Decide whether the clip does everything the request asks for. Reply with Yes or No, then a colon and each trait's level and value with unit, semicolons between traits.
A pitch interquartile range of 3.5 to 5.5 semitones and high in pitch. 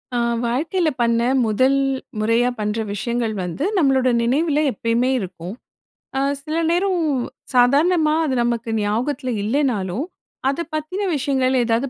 Yes: average, 4.5 semitones; very high, 255 Hz